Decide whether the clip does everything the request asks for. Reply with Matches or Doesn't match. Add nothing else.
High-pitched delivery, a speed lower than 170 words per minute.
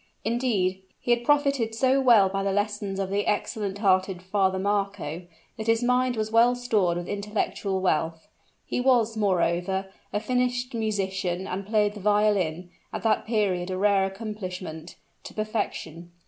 Matches